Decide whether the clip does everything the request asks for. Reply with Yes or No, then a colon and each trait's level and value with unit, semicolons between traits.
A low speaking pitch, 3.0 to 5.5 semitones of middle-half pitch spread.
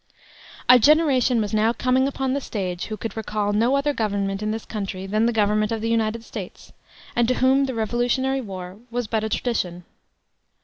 No: high, 225 Hz; average, 3.3 semitones